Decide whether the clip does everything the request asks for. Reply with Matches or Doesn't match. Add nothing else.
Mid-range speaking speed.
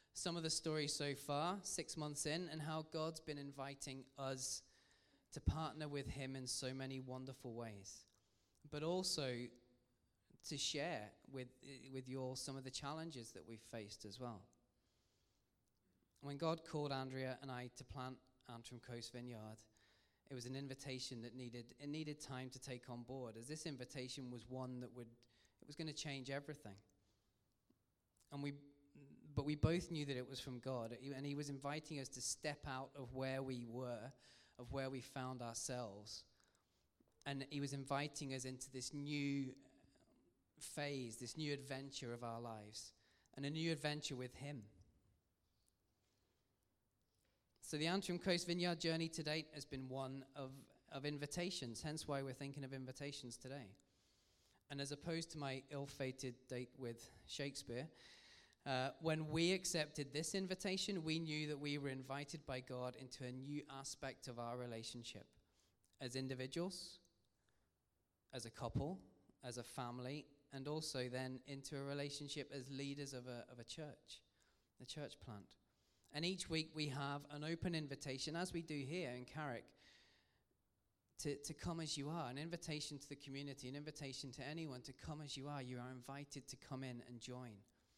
Matches